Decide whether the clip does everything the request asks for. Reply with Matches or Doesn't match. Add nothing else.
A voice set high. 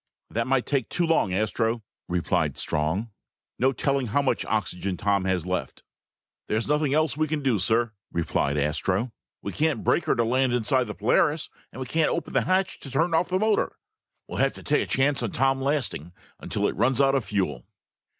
Doesn't match